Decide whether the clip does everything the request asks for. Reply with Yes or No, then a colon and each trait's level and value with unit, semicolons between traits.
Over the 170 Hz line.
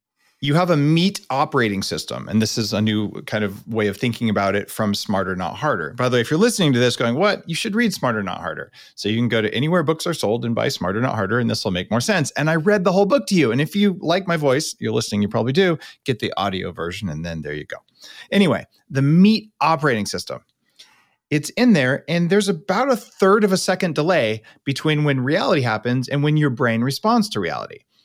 No: medium, 140 Hz